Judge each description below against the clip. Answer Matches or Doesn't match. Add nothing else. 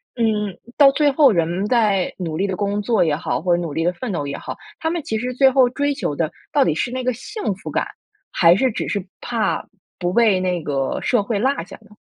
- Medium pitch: Doesn't match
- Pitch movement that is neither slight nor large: Doesn't match